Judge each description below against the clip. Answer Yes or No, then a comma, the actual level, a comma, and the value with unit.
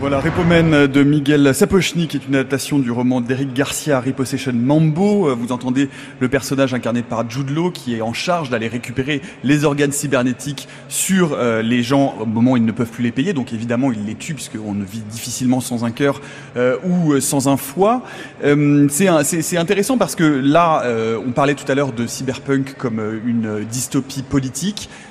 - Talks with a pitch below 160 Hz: Yes, low, 135 Hz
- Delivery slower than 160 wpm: No, average, 195 wpm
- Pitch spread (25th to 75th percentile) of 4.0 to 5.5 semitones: No, average, 3.0 semitones